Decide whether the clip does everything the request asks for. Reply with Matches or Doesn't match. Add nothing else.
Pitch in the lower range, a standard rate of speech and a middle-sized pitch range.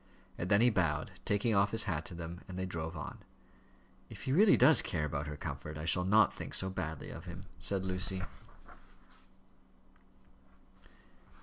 Matches